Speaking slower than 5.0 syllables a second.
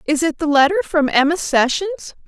No: 6.1 syllables/s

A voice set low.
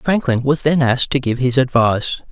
Yes: low, 130 Hz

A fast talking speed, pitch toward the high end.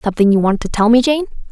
Yes: fast, 275 wpm; high, 230 Hz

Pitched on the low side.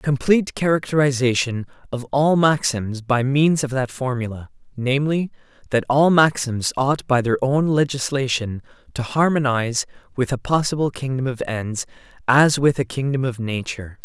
Yes: low, 130 Hz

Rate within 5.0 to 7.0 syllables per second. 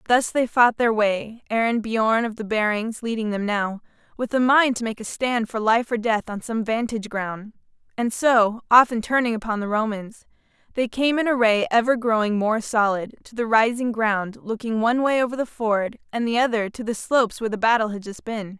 Yes: 5.2 syllables/s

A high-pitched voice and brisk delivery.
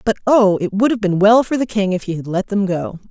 Yes: high, 200 Hz; fast, 310 wpm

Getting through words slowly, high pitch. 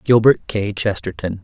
No: slow, 125 wpm; low, 105 Hz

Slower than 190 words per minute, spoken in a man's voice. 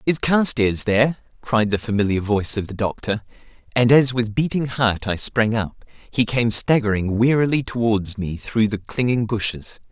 Yes: average, 170 wpm; male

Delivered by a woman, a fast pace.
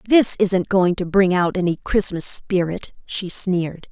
No: female; average, 170 wpm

